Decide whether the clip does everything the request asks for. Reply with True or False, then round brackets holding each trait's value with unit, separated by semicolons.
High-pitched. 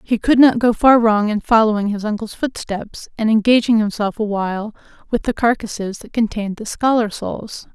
True (220 Hz)